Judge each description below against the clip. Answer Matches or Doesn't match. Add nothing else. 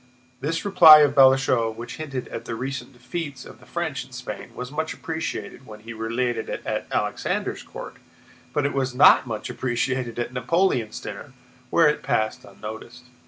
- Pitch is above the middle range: Doesn't match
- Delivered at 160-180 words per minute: Matches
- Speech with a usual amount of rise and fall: Matches